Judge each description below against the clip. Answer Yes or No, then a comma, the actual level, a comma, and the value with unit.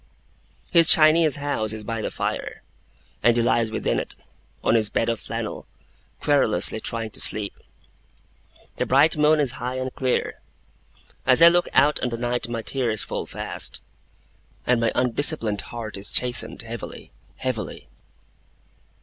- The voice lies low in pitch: Yes, low, 120 Hz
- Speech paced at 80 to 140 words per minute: No, average, 150 wpm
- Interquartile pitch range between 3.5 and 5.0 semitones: Yes, average, 3.9 semitones